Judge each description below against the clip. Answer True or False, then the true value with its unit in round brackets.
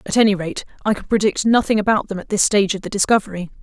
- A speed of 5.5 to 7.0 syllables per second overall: False (7.2 syllables/s)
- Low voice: False (205 Hz)